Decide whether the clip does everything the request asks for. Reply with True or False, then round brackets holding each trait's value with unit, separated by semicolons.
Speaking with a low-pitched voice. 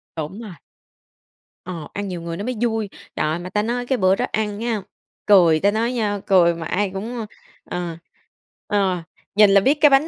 False (205 Hz)